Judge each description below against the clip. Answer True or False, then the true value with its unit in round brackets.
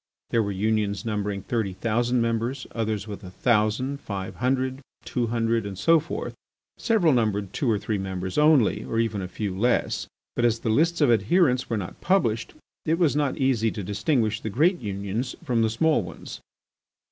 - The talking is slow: False (180 wpm)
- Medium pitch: False (115 Hz)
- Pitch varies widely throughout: False (3.9 semitones)